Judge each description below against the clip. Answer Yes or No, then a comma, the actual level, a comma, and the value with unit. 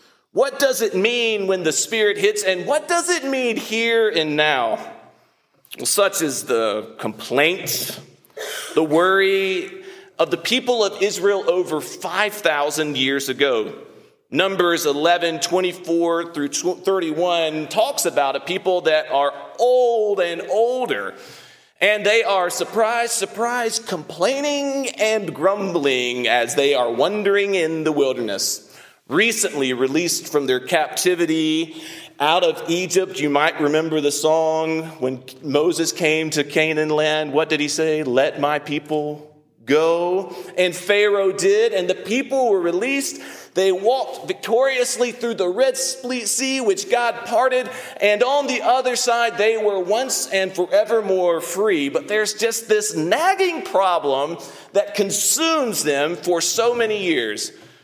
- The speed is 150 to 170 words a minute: No, slow, 135 wpm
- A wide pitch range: Yes, wide, 7.5 semitones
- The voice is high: Yes, high, 195 Hz